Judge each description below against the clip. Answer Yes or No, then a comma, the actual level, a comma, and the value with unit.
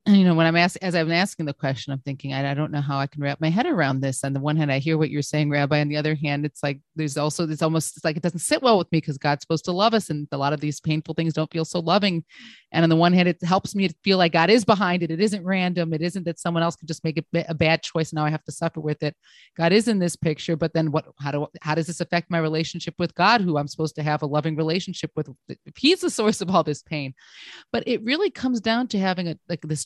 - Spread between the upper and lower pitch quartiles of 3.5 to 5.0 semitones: No, average, 2.8 semitones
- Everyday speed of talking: No, fast, 305 wpm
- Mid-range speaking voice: Yes, medium, 165 Hz